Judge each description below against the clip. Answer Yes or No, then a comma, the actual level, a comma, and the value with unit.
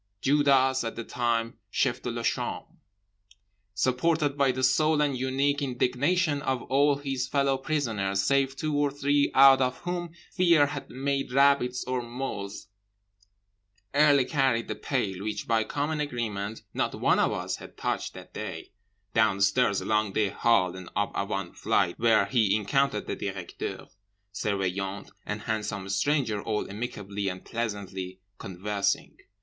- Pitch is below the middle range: Yes, low, 125 Hz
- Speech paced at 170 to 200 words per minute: No, average, 140 wpm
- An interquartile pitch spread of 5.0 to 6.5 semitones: Yes, average, 5.3 semitones